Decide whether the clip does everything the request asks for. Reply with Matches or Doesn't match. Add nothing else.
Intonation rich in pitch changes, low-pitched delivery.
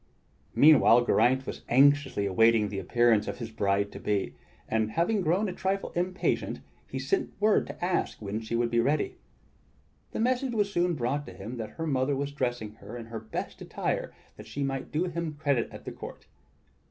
Matches